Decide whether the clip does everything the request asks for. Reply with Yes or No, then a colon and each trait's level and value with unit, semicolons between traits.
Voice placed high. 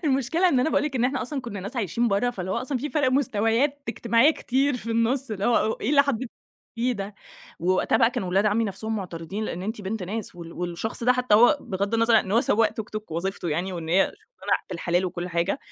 Yes: high, 225 Hz